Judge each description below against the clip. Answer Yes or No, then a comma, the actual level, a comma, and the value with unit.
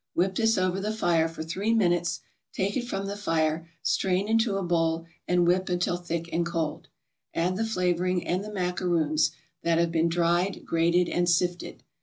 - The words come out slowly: No, average, 180 wpm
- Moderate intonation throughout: No, narrow, 2.3 semitones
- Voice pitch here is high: No, medium, 175 Hz